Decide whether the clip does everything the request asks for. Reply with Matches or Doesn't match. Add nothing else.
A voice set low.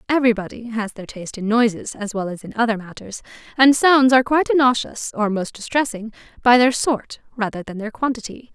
Doesn't match